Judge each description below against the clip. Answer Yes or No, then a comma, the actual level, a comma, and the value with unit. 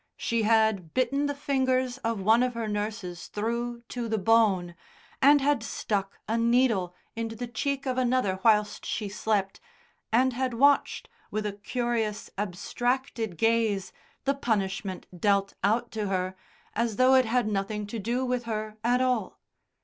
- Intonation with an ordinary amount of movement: Yes, average, 3.3 semitones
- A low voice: No, high, 225 Hz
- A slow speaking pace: No, average, 155 wpm